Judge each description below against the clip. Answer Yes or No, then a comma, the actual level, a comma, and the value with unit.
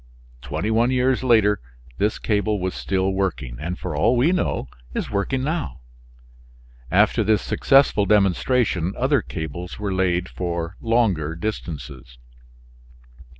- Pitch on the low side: Yes, low, 100 Hz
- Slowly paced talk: Yes, slow, 125 wpm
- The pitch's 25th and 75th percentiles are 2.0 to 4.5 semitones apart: No, average, 4.9 semitones